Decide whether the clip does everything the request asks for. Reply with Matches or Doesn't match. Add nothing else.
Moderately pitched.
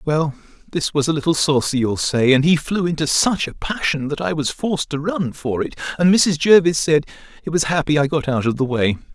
Matches